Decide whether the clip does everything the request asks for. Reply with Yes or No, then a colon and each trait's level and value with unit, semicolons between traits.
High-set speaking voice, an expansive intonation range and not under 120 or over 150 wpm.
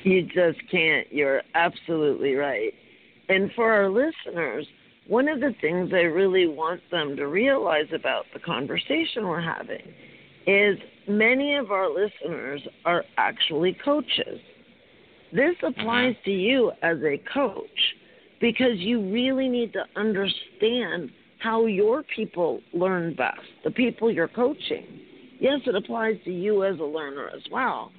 Yes: high, 215 Hz; wide, 5.9 semitones; average, 140 wpm